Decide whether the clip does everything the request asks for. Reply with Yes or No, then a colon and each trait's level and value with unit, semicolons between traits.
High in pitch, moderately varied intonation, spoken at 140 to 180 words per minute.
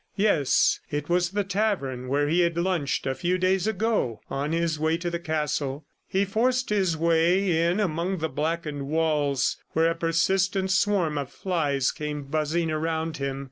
No: medium, 165 Hz; average, 3.7 semitones; average, 170 wpm